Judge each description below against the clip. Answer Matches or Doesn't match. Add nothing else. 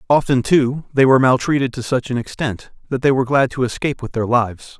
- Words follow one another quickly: Matches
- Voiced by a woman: Doesn't match